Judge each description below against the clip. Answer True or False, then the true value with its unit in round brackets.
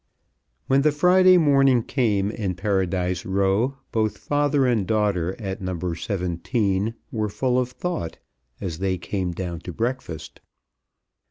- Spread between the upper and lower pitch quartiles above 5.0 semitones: True (5.6 semitones)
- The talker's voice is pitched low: True (105 Hz)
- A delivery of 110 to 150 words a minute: True (135 wpm)